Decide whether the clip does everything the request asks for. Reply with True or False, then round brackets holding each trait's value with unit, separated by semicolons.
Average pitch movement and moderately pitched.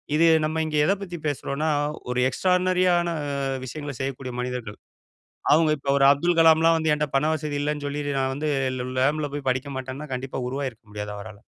True (3.2 semitones; 145 Hz)